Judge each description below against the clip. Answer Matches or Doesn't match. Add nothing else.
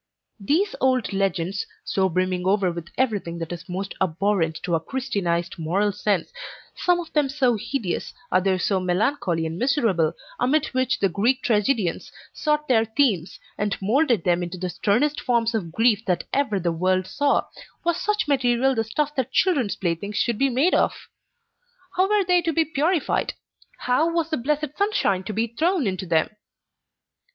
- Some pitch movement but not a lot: Doesn't match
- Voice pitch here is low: Doesn't match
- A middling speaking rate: Matches